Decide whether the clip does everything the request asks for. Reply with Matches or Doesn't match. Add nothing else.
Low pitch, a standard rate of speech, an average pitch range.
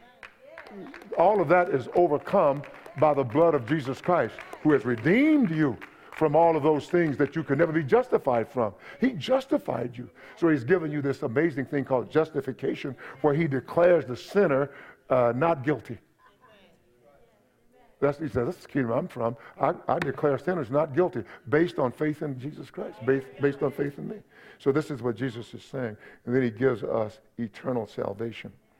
Doesn't match